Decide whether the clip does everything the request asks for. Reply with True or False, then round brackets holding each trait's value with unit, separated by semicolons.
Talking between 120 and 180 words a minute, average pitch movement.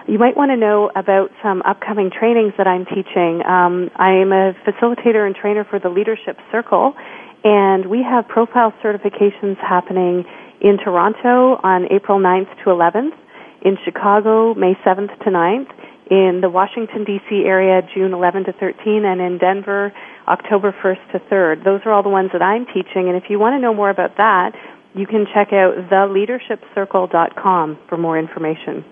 False (170 wpm; 2.3 semitones)